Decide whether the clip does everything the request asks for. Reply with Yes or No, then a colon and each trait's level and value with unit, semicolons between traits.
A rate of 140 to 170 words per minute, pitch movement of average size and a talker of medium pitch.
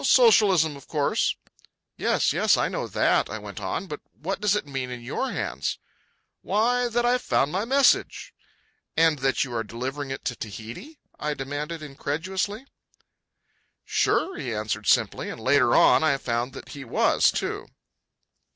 No: average, 160 wpm; wide, 7.7 semitones; medium, 145 Hz